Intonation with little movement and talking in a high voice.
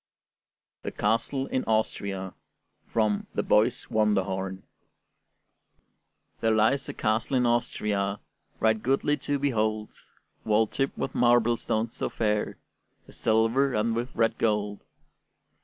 No: narrow, 2.2 semitones; low, 110 Hz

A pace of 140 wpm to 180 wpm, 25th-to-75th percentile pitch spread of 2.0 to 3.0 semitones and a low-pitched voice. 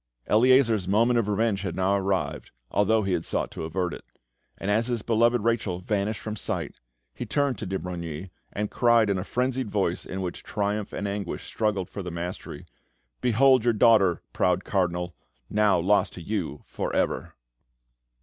No: average, 175 wpm; average, 3.6 semitones; low, 100 Hz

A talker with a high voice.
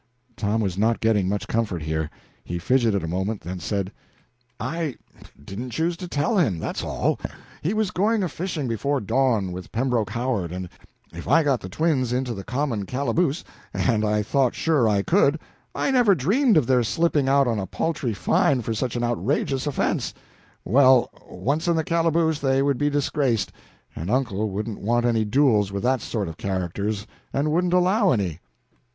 No: low, 125 Hz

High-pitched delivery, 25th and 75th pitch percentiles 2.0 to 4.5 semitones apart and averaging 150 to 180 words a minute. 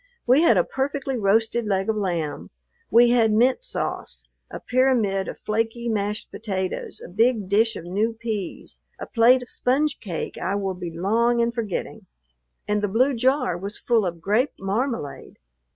Yes: high, 220 Hz; average, 3.7 semitones; average, 170 wpm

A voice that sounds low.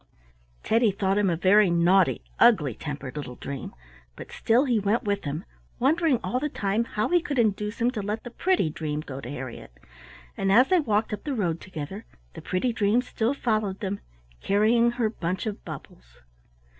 No: high, 205 Hz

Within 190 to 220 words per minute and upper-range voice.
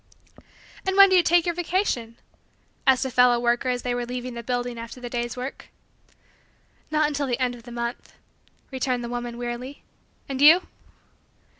No: average, 175 wpm; very high, 250 Hz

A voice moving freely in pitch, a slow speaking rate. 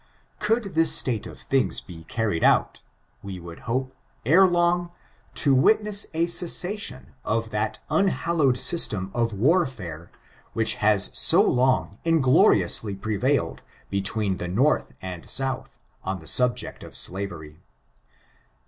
Yes: wide, 8.9 semitones; slow, 130 wpm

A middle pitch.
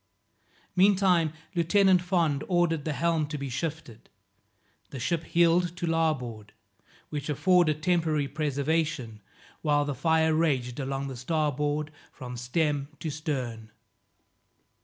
Yes: medium, 155 Hz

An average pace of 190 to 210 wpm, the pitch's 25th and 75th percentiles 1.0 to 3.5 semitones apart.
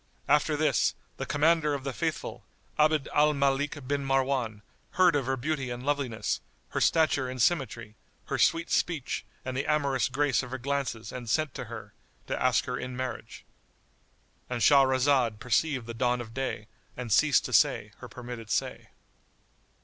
No: average, 165 wpm; average, 2.8 semitones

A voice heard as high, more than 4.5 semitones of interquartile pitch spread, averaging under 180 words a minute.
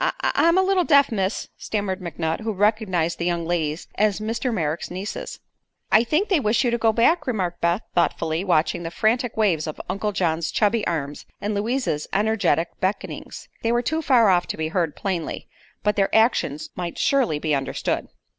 No: high, 200 Hz; average, 5.1 semitones; average, 185 wpm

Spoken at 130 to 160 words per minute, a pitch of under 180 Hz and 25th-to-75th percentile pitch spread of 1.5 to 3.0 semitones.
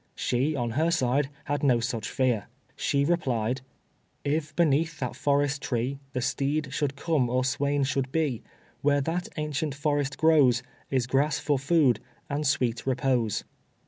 Yes: average, 150 wpm; medium, 140 Hz; average, 2.7 semitones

